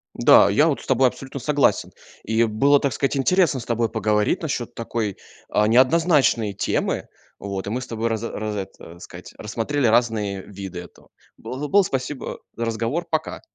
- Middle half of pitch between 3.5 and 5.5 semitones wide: Yes, average, 4.6 semitones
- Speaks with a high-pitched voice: No, low, 115 Hz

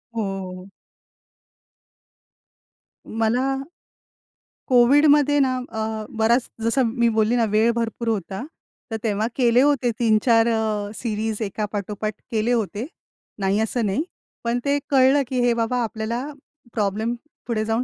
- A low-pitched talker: No, high, 225 Hz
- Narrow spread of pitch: Yes, narrow, 2.3 semitones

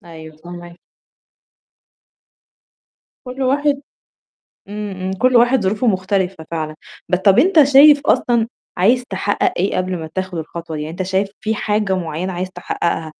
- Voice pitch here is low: No, high, 190 Hz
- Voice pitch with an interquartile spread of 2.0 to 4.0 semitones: No, average, 5.2 semitones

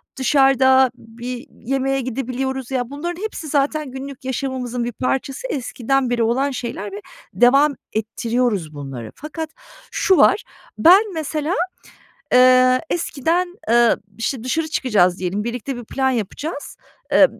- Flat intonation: No, average, 3.0 semitones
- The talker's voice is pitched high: Yes, very high, 260 Hz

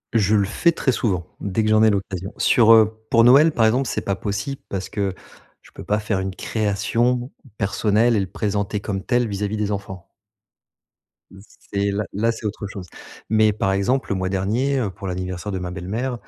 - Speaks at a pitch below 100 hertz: No, low, 105 Hz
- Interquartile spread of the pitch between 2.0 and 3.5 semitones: Yes, average, 2.7 semitones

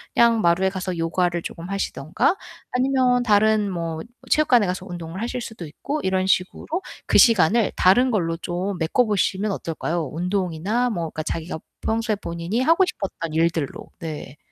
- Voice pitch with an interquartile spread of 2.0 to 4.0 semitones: No, average, 5.1 semitones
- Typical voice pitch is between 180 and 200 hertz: Yes, high, 190 Hz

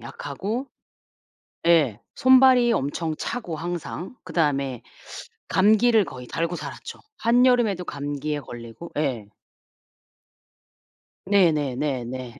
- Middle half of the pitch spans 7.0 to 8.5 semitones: Yes, wide, 8.0 semitones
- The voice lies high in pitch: No, medium, 165 Hz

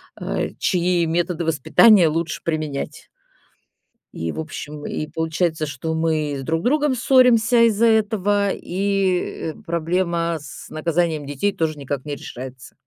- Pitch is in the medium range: Yes, medium, 165 Hz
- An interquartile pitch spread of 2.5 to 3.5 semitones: No, average, 4.3 semitones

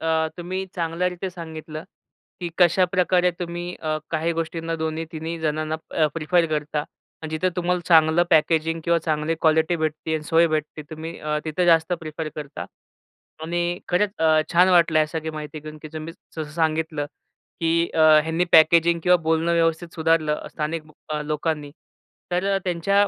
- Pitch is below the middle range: No, medium, 160 Hz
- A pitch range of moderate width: No, narrow, 1.5 semitones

